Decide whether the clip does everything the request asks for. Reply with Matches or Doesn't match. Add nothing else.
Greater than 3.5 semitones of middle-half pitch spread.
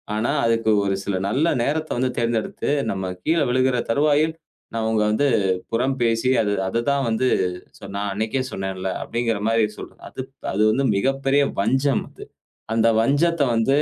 Matches